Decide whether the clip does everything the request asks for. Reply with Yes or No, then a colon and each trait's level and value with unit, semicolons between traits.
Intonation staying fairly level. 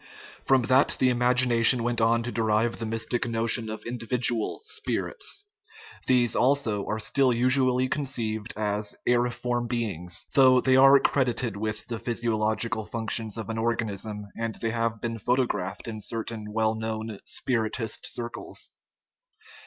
Yes: narrow, 2.1 semitones